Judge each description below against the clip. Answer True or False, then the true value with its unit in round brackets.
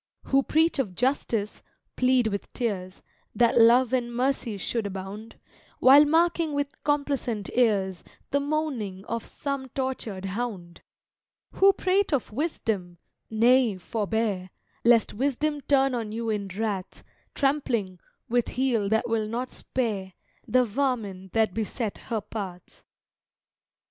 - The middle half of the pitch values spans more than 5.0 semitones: False (4.7 semitones)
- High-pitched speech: True (230 Hz)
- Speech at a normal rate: False (125 wpm)